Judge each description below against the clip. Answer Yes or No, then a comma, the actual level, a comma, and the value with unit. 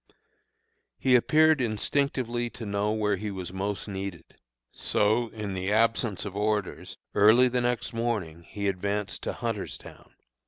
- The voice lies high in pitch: No, low, 105 Hz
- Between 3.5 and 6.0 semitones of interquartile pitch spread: No, average, 3.1 semitones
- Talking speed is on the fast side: No, slow, 135 wpm